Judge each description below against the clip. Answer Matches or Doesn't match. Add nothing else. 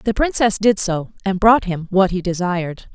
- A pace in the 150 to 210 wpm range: Matches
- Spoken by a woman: Matches